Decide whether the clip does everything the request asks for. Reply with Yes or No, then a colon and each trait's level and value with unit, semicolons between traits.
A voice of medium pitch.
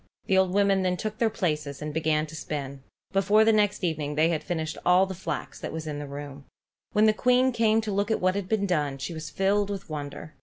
Yes: medium, 180 Hz